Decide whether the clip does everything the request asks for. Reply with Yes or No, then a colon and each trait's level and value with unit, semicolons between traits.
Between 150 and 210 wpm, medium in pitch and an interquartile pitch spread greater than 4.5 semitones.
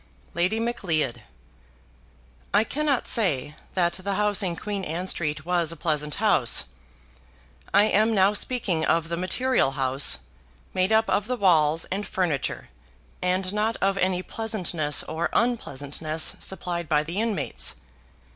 No: slow, 135 wpm; medium, 180 Hz; average, 4.9 semitones